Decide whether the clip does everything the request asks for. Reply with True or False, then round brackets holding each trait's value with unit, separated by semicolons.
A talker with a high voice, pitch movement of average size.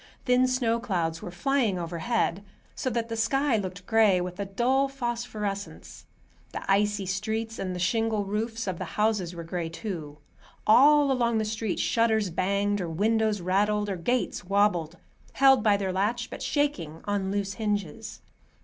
True (210 Hz; 3.6 semitones)